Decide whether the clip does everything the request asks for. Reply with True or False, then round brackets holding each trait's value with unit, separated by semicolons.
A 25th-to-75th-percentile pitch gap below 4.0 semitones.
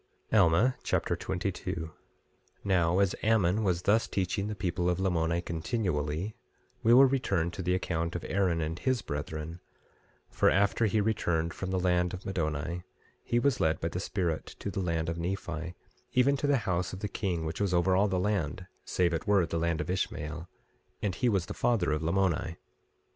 True (3.2 semitones)